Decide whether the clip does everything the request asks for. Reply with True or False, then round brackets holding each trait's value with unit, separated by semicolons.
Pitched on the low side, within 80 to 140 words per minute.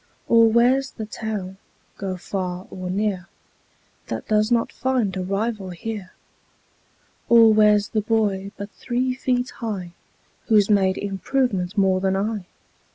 False (210 Hz; 135 wpm)